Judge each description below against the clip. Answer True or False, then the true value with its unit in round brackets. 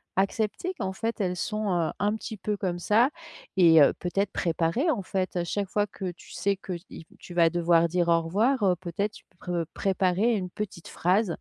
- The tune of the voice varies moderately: True (3.2 semitones)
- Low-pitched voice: False (190 Hz)